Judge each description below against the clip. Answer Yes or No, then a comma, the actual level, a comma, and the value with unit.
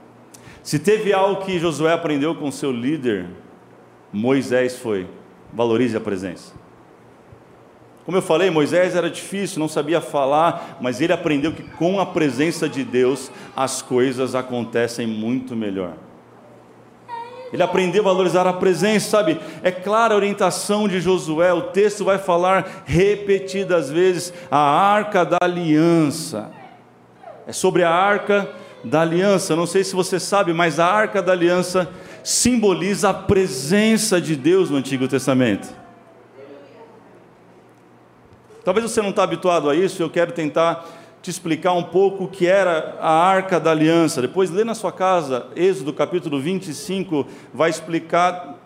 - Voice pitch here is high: No, medium, 170 Hz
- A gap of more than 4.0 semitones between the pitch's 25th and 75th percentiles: Yes, average, 4.6 semitones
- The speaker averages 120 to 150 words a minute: Yes, average, 140 wpm